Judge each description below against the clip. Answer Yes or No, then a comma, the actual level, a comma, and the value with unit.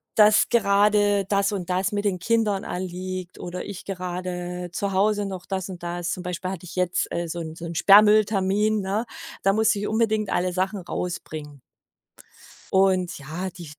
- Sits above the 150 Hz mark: Yes, high, 190 Hz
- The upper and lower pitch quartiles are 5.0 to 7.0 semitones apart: No, narrow, 2.4 semitones